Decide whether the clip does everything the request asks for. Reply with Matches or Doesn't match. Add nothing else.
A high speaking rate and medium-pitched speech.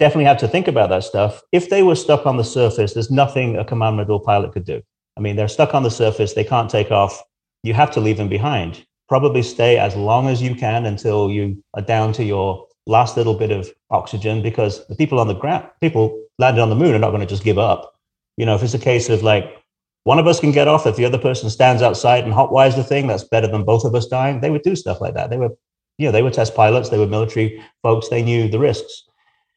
Doesn't match